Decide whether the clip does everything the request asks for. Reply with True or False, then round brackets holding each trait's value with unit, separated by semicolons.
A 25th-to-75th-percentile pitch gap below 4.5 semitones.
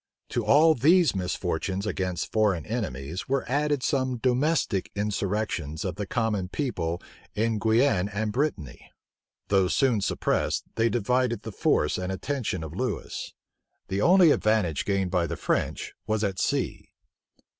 False (5.3 semitones)